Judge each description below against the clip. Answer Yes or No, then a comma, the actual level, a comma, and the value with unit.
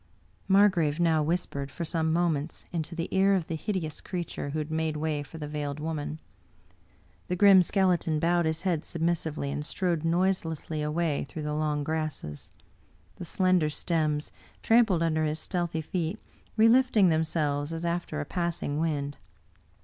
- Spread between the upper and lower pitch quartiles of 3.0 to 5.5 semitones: No, narrow, 2.5 semitones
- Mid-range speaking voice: Yes, medium, 160 Hz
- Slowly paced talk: No, average, 165 wpm